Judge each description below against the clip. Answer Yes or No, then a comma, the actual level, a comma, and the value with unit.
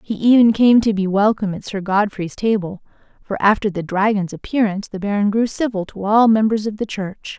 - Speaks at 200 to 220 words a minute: Yes, fast, 205 wpm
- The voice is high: Yes, high, 205 Hz